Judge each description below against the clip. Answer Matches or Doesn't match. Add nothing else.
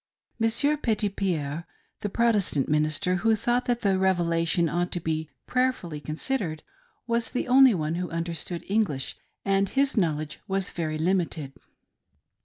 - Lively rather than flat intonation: Matches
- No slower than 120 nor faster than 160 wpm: Matches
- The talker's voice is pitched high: Doesn't match